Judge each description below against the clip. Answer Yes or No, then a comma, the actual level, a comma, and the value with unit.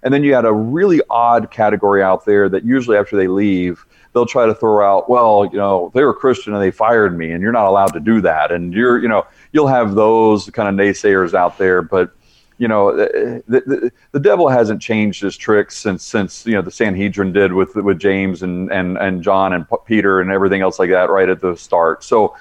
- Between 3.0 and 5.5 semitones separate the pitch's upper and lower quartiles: No, narrow, 2.6 semitones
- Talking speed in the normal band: No, fast, 230 wpm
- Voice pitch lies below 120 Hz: Yes, low, 100 Hz